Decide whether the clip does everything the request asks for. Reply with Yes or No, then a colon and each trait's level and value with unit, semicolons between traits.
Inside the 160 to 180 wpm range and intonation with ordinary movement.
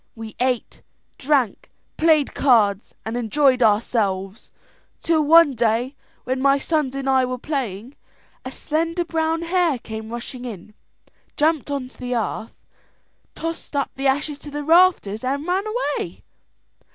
No: average, 140 wpm; average, 4.9 semitones